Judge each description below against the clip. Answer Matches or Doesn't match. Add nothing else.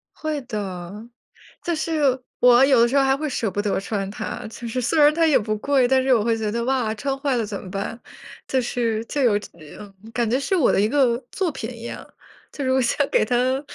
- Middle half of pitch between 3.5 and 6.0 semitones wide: Matches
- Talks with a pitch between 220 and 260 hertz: Matches